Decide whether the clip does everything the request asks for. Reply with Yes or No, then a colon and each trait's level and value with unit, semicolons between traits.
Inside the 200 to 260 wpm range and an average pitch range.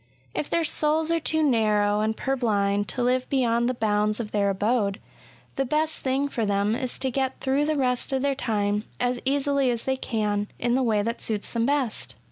Yes: fast, 205 wpm; average, 4.3 semitones